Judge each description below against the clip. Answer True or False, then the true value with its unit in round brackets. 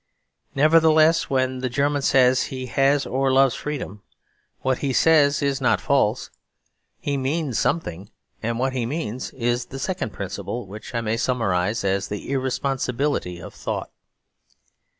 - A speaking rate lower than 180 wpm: True (145 wpm)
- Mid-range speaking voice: False (130 Hz)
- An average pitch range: True (3.2 semitones)